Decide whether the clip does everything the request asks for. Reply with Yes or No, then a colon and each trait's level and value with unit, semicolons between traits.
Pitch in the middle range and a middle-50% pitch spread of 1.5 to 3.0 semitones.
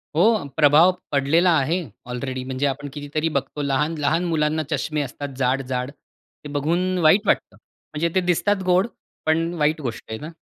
No: medium, 150 Hz; average, 3.5 semitones